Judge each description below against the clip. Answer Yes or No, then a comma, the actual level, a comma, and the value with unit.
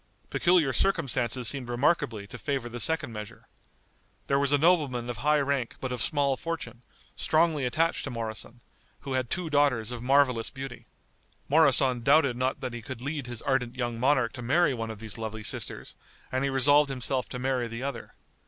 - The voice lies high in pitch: No, low, 130 Hz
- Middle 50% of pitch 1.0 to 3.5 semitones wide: Yes, average, 3.1 semitones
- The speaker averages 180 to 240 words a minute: Yes, average, 185 wpm